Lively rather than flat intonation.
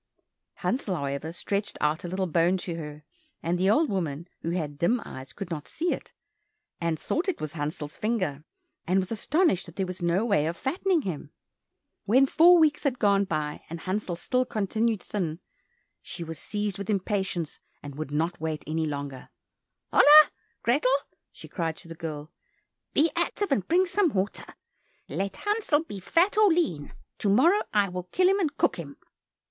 Yes: wide, 7.9 semitones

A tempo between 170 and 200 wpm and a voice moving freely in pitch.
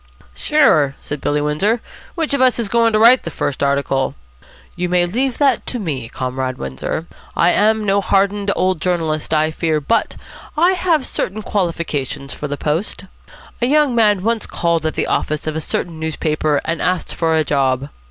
Yes: average, 180 wpm; wide, 6.6 semitones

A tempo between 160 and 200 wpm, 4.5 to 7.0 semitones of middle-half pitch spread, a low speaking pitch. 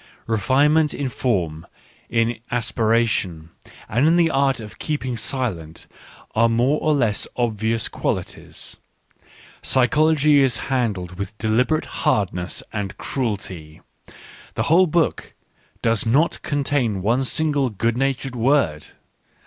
No: slow, 135 wpm; average, 4.9 semitones; low, 120 Hz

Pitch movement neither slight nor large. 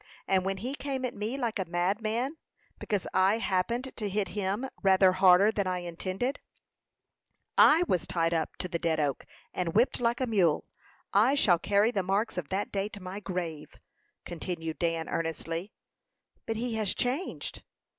Yes: average, 4.2 semitones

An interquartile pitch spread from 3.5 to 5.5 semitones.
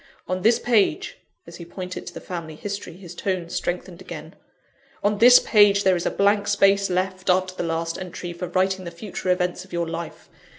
No: narrow, 2.5 semitones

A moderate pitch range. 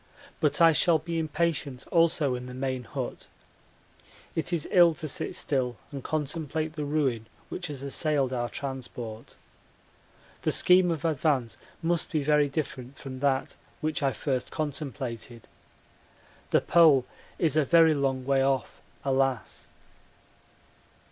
Yes: average, 3.3 semitones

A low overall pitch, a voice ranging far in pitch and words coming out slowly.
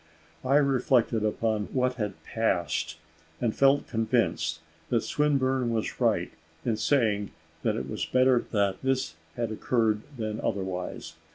No: low, 115 Hz; average, 3.3 semitones; slow, 125 wpm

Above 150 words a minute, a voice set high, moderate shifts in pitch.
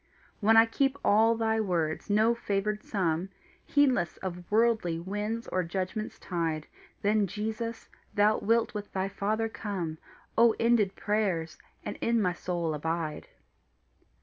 No: slow, 135 wpm; high, 205 Hz; average, 4.0 semitones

